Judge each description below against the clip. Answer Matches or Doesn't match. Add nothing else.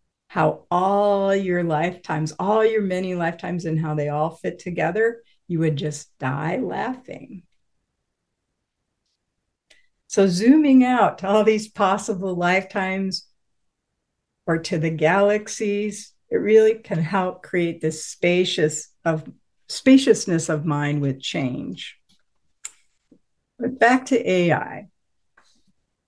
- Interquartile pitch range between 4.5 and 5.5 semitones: Matches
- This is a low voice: Doesn't match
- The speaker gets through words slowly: Matches